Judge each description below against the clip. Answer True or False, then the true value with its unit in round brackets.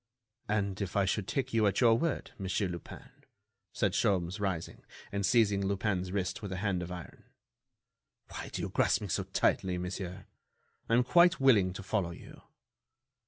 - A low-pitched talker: True (100 Hz)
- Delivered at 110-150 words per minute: False (170 wpm)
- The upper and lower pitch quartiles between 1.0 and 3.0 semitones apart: True (2.6 semitones)